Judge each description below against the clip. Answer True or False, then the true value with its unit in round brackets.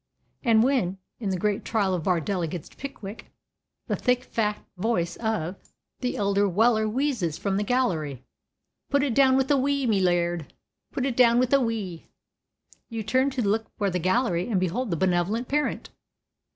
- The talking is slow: False (175 wpm)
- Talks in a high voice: True (215 Hz)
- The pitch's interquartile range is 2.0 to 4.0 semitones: False (5.4 semitones)